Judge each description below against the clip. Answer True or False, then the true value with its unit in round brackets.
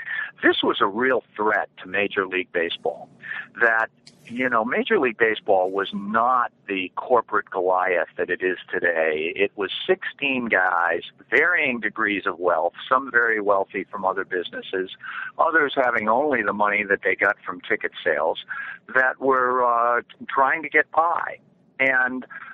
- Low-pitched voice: True (130 Hz)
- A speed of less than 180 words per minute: True (150 wpm)